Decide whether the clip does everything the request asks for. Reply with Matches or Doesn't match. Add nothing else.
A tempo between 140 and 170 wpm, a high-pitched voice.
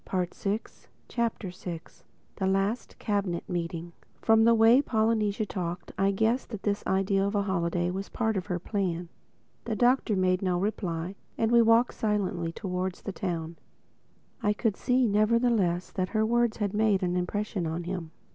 Matches